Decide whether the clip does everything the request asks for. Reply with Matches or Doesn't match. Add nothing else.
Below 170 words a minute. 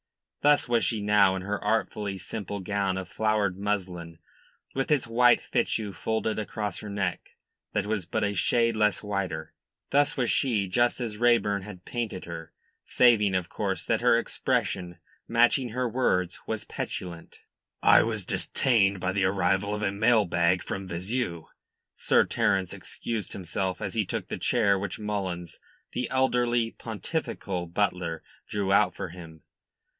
Matches